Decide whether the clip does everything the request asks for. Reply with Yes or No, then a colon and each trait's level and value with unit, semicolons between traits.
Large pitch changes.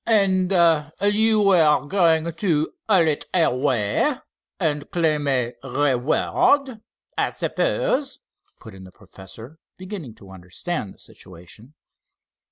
Yes: wide, 8.2 semitones